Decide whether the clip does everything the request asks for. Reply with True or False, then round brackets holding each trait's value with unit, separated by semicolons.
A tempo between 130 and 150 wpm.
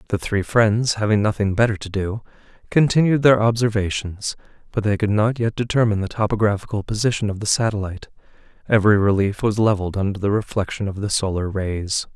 False (170 wpm)